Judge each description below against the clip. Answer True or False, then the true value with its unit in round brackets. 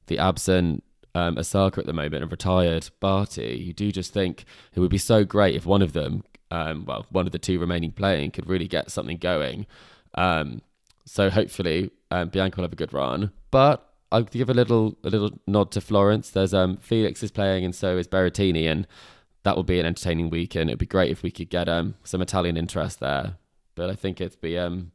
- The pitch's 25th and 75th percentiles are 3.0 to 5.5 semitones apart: False (2.6 semitones)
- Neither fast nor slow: False (215 wpm)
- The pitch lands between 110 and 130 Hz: False (95 Hz)